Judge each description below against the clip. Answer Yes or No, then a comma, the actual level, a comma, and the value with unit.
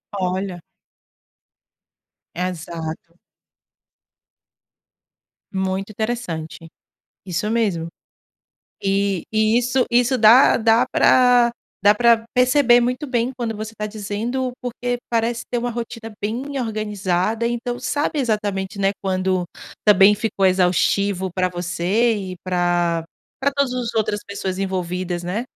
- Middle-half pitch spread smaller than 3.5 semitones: No, average, 4.4 semitones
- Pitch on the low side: No, high, 210 Hz